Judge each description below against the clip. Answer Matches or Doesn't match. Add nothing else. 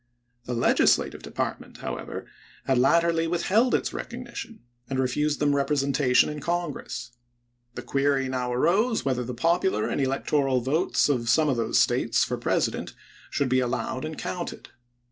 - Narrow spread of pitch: Doesn't match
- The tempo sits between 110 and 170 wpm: Matches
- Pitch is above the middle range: Doesn't match